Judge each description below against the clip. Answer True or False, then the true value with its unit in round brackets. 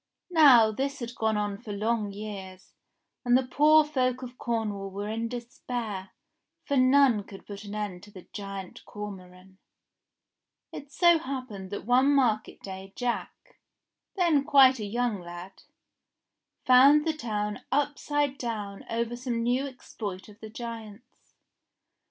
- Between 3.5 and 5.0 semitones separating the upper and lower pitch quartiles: True (4.3 semitones)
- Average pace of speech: True (145 wpm)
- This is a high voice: True (230 Hz)